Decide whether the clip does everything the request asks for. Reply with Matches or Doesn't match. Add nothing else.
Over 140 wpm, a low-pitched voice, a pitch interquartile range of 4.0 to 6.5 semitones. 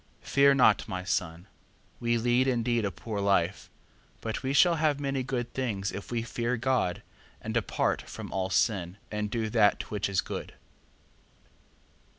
Matches